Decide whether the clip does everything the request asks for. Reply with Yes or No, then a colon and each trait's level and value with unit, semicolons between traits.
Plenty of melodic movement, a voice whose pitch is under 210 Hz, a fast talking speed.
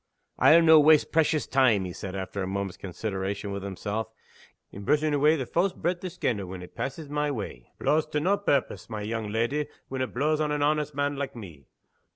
Yes: wide, 7.1 semitones; low, 135 Hz; fast, 210 wpm